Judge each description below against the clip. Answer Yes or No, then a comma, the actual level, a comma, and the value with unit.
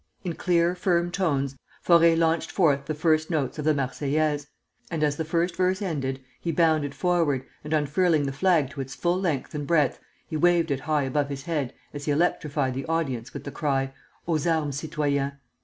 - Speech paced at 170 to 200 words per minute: Yes, average, 190 wpm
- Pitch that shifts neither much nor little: Yes, average, 3.2 semitones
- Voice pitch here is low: No, medium, 155 Hz